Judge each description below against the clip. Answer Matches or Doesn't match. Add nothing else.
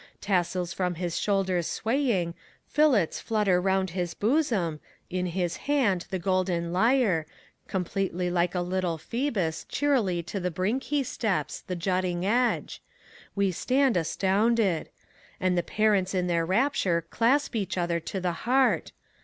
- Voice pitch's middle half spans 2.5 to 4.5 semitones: Matches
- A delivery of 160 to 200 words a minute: Doesn't match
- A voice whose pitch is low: Doesn't match